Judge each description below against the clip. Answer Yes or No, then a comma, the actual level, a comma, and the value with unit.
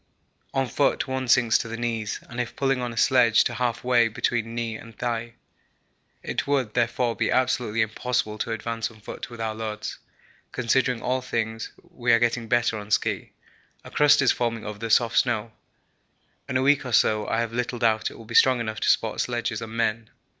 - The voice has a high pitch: No, low, 115 Hz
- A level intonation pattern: Yes, narrow, 1.8 semitones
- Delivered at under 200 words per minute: No, fast, 205 wpm